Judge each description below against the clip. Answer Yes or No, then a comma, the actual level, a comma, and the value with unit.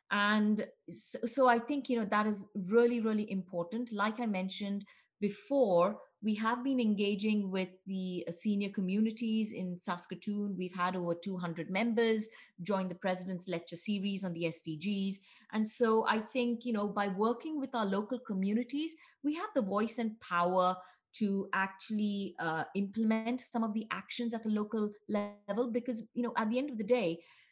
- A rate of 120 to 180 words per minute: Yes, average, 170 wpm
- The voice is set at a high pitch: Yes, high, 210 Hz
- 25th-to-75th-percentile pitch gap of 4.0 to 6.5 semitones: No, average, 3.3 semitones